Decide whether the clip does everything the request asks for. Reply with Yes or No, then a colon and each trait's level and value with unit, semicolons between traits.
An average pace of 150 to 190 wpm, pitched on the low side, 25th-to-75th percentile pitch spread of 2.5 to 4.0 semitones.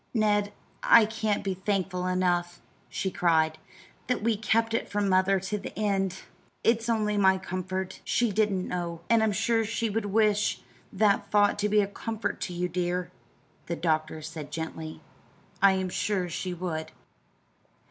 No: average, 160 wpm; high, 195 Hz; average, 2.9 semitones